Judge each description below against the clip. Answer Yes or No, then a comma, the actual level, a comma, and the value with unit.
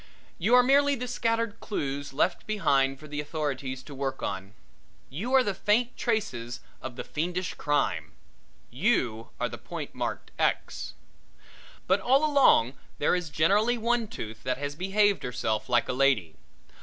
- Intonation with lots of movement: Yes, wide, 9.0 semitones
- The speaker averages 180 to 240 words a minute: No, average, 155 wpm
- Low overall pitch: No, medium, 155 Hz